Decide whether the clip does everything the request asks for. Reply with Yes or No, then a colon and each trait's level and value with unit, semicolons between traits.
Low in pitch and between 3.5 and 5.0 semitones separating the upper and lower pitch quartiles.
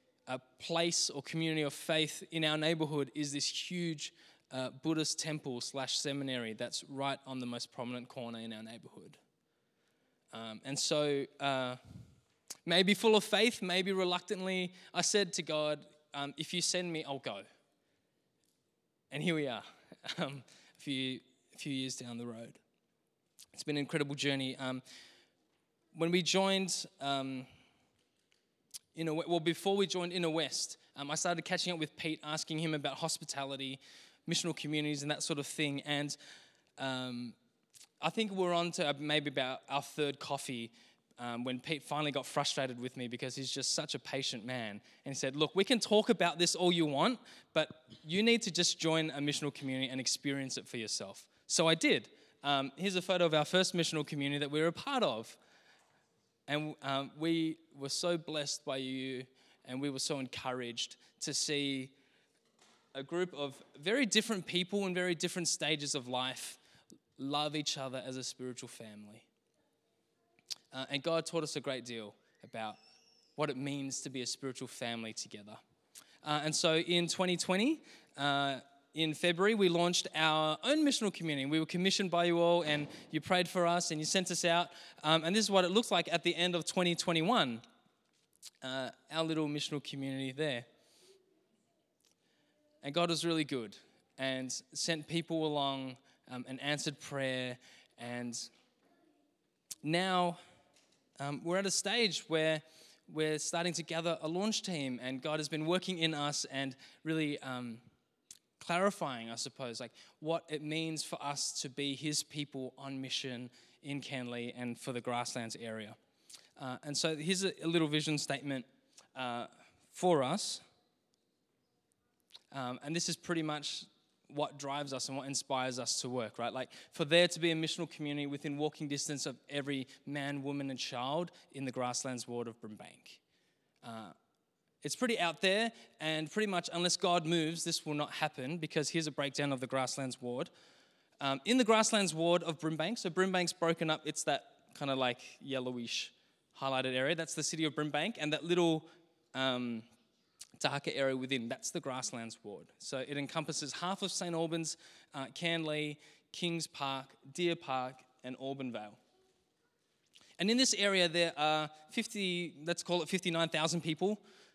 No: medium, 150 Hz; average, 4.2 semitones